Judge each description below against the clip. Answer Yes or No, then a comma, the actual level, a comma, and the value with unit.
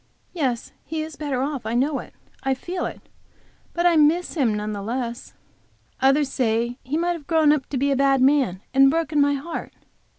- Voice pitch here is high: Yes, very high, 275 Hz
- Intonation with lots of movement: No, average, 3.6 semitones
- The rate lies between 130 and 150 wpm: No, average, 200 wpm